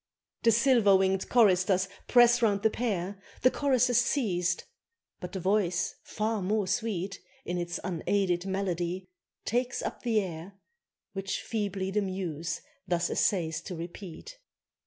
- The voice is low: No, high, 195 Hz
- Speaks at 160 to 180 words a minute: No, slow, 135 wpm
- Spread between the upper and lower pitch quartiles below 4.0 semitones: Yes, average, 3.6 semitones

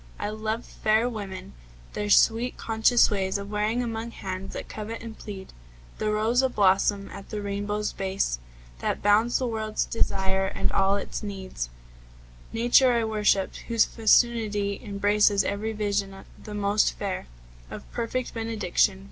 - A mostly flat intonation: Yes, narrow, 2.2 semitones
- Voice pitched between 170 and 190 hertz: No, high, 210 Hz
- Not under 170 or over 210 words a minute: No, average, 145 wpm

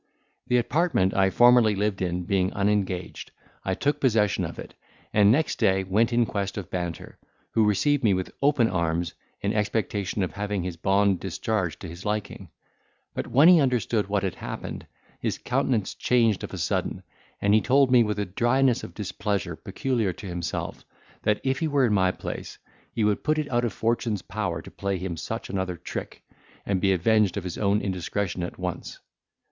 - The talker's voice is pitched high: No, low, 105 Hz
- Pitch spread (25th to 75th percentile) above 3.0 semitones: Yes, average, 4.1 semitones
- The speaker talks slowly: No, average, 185 wpm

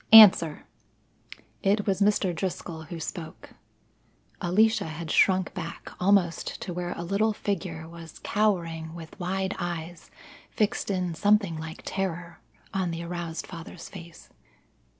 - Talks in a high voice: No, medium, 175 Hz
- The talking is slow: Yes, slow, 130 wpm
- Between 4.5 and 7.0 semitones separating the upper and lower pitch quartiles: No, average, 2.9 semitones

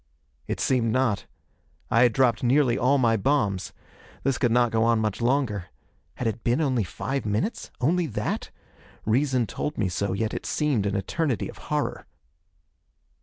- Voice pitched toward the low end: Yes, low, 120 Hz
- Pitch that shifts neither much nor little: Yes, average, 3.9 semitones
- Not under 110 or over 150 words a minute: No, average, 165 wpm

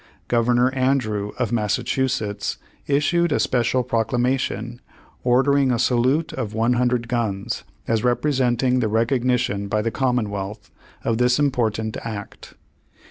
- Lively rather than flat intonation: No, narrow, 2.5 semitones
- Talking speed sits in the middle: No, slow, 125 wpm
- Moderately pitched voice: No, low, 120 Hz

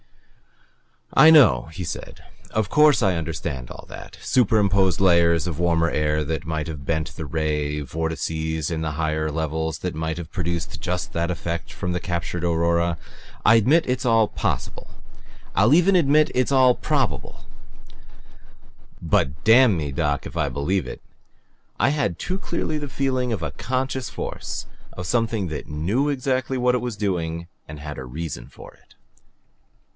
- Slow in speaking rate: No, average, 160 wpm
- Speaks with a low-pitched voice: Yes, very low, 85 Hz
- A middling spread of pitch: No, wide, 7.5 semitones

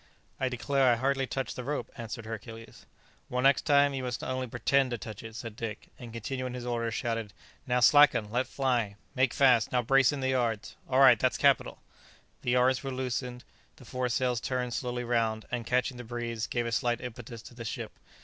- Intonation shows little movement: Yes, narrow, 2.0 semitones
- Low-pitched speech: Yes, low, 125 Hz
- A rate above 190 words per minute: Yes, average, 200 wpm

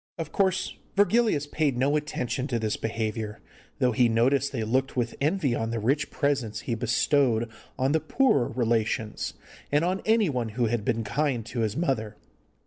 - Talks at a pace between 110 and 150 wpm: No, average, 170 wpm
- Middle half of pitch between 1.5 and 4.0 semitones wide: No, average, 4.4 semitones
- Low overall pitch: Yes, low, 125 Hz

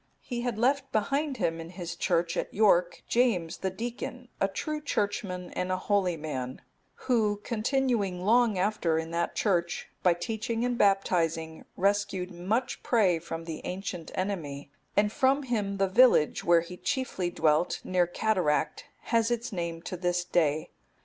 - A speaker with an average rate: Yes, average, 155 wpm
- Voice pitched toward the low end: No, high, 190 Hz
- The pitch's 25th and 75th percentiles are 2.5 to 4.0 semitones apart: No, average, 4.9 semitones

